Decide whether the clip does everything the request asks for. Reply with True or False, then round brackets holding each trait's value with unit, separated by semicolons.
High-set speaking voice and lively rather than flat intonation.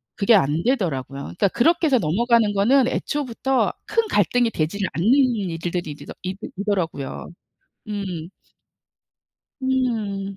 True (205 Hz; 6.2 semitones)